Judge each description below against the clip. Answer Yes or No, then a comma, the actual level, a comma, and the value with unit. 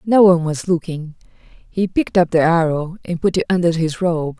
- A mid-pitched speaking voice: Yes, medium, 170 Hz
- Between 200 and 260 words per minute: Yes, fast, 205 wpm